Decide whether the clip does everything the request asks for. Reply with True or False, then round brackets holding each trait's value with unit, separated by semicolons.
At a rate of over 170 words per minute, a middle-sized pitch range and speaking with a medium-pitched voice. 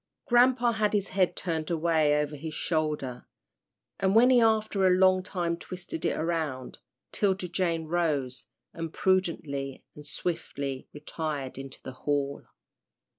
False (135 wpm; 4.2 semitones; 165 Hz)